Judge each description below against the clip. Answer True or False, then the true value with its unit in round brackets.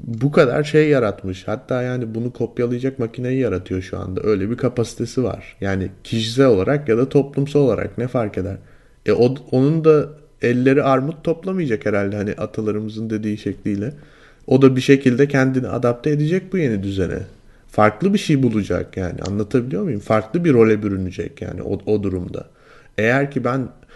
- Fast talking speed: True (165 wpm)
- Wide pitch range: False (4.9 semitones)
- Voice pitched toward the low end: True (120 Hz)